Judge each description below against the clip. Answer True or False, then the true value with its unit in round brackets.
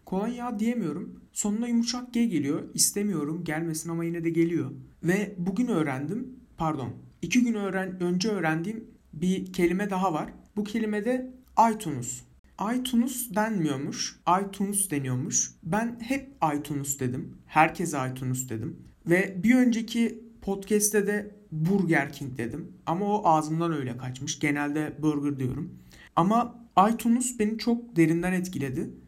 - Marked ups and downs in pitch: True (6.4 semitones)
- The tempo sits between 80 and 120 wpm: False (130 wpm)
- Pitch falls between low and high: True (180 Hz)